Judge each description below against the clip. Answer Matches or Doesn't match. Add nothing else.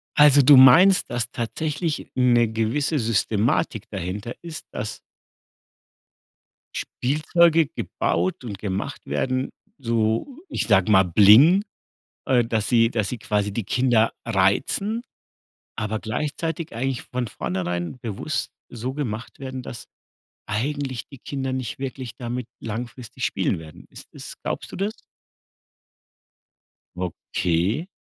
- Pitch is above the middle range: Doesn't match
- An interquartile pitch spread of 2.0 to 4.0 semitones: Doesn't match